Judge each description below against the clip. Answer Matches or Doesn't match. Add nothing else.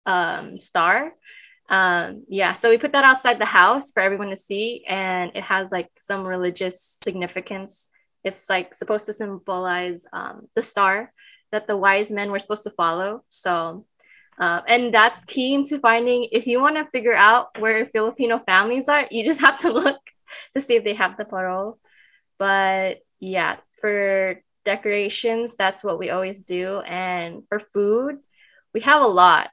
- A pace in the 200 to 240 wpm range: Doesn't match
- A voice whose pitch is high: Matches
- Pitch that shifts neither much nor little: Matches